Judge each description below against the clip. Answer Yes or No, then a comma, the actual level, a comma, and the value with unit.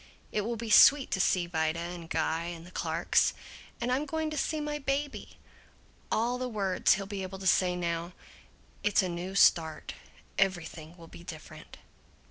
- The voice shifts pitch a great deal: Yes, wide, 5.7 semitones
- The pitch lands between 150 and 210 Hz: Yes, high, 190 Hz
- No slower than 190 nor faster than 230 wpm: No, average, 175 wpm